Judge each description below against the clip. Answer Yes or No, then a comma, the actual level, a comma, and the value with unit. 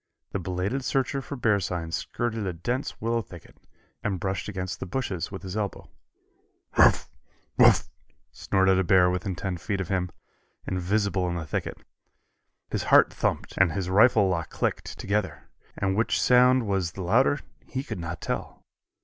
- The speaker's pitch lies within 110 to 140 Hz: No, very low, 95 Hz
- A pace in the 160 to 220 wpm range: Yes, average, 165 wpm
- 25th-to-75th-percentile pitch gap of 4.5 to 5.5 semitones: No, average, 3.7 semitones